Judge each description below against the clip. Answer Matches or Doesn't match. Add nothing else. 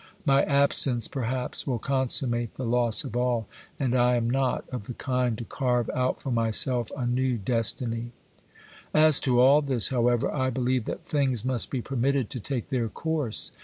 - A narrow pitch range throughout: Matches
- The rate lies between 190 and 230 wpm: Doesn't match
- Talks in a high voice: Doesn't match